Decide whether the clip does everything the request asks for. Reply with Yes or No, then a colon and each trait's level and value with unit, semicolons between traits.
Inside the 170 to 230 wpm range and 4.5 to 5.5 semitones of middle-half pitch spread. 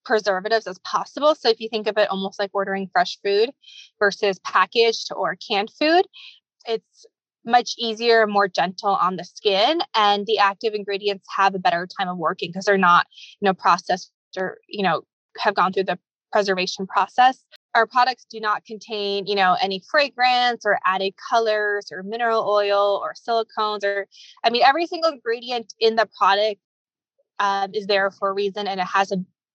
No: average, 180 wpm; average, 3.1 semitones